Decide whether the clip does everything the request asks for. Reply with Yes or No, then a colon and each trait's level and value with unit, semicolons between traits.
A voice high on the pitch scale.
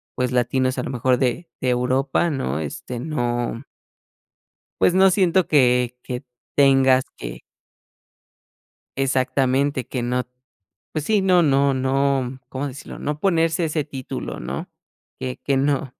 No: low, 135 Hz